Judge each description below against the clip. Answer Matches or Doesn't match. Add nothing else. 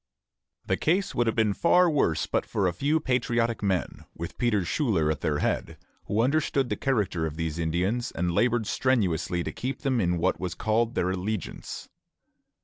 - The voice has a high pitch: Doesn't match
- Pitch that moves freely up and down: Matches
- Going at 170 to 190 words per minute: Matches